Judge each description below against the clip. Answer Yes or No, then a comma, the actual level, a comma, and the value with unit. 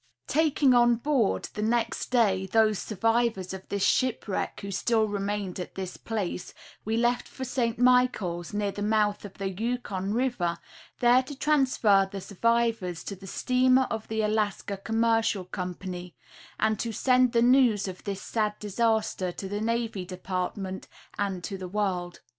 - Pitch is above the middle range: Yes, high, 215 Hz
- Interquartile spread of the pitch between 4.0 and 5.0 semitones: No, average, 3.5 semitones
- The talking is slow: No, average, 160 wpm